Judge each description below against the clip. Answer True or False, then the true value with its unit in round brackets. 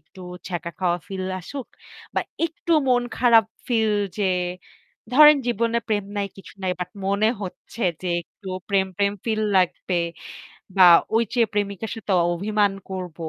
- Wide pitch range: False (3.3 semitones)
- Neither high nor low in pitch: False (205 Hz)